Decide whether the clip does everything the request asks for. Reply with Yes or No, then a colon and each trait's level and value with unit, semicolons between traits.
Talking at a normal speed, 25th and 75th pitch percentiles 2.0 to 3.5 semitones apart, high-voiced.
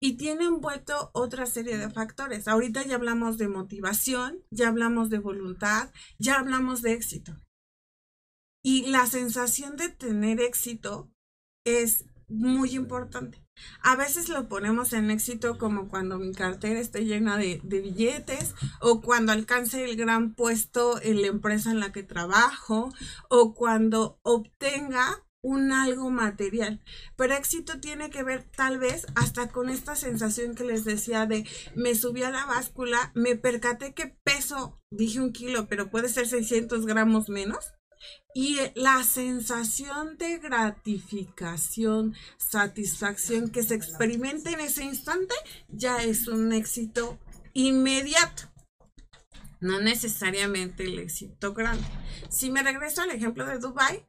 Yes: average, 140 wpm; average, 3.2 semitones; high, 235 Hz